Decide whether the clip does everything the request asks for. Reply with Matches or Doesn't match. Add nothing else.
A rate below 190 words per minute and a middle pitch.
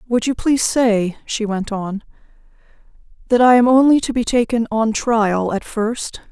Doesn't match